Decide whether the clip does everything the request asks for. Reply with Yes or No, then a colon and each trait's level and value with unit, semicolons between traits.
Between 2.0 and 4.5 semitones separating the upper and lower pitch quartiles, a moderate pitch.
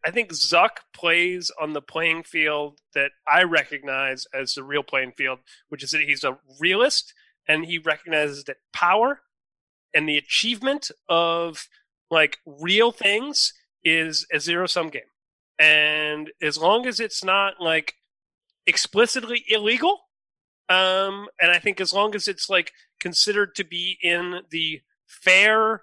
No: average, 5.2 semitones; medium, 170 Hz